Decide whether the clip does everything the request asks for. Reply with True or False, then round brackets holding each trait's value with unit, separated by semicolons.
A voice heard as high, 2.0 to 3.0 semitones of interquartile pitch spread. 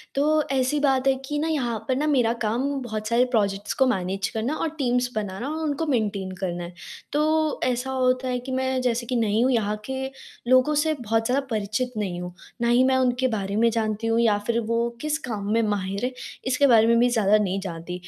False (235 Hz; 3.8 semitones)